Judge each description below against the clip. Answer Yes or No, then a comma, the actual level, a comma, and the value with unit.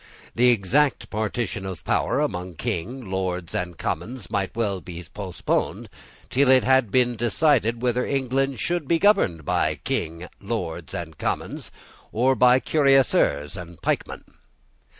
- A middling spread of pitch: No, wide, 6.4 semitones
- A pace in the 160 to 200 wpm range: No, slow, 135 wpm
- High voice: No, low, 115 Hz